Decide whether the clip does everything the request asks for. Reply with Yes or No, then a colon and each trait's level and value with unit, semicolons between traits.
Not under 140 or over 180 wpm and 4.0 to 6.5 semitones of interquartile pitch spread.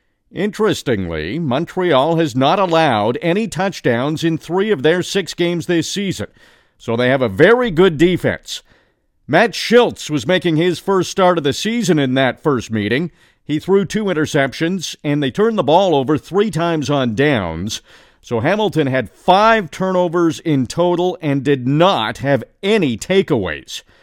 Yes: average, 155 wpm; average, 4.8 semitones